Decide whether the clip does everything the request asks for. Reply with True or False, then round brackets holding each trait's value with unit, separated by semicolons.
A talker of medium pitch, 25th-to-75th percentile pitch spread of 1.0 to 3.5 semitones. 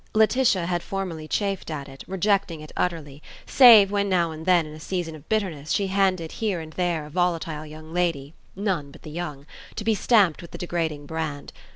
False (170 Hz; 3.9 semitones)